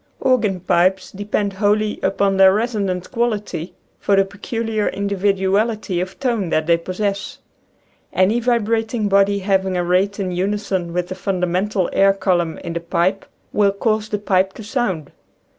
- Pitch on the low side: No, high, 195 Hz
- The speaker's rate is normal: Yes, average, 155 wpm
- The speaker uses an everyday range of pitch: No, narrow, 2.2 semitones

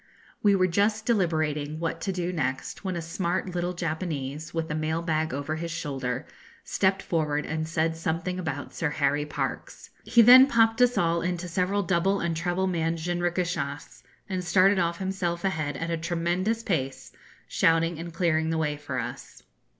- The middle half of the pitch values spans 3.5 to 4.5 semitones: No, narrow, 2.6 semitones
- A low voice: No, medium, 170 Hz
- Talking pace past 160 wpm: Yes, average, 175 wpm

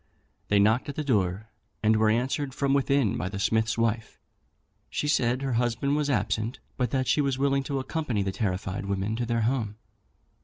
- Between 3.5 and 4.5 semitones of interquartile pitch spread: Yes, average, 4.1 semitones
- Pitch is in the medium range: No, low, 120 Hz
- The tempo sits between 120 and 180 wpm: No, average, 190 wpm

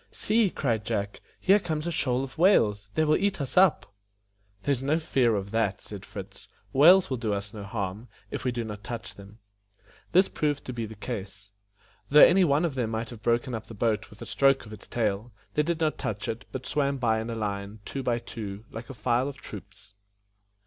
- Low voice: Yes, low, 120 Hz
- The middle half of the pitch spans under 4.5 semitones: No, average, 5.1 semitones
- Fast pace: Yes, fast, 220 wpm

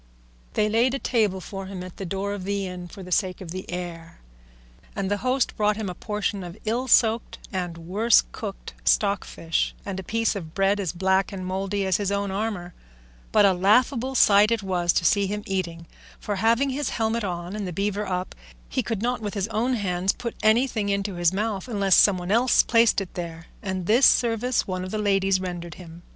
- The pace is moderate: No, fast, 210 wpm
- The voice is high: Yes, high, 200 Hz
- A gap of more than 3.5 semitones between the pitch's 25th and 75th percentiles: No, average, 3.0 semitones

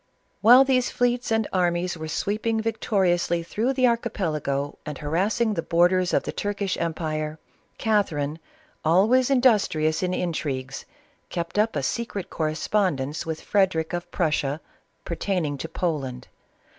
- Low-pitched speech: No, medium, 175 Hz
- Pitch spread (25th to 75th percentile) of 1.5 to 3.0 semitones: No, average, 5.3 semitones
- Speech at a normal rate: No, slow, 130 wpm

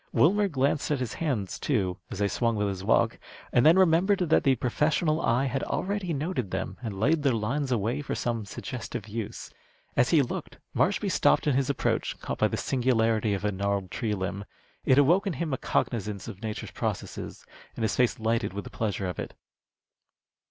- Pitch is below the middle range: Yes, low, 120 Hz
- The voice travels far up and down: Yes, wide, 6.0 semitones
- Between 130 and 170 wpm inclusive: No, average, 195 wpm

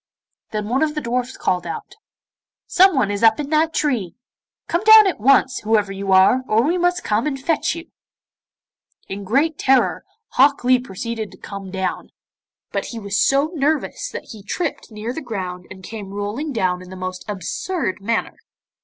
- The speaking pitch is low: No, high, 230 Hz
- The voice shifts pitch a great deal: Yes, wide, 6.8 semitones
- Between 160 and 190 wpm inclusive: Yes, average, 180 wpm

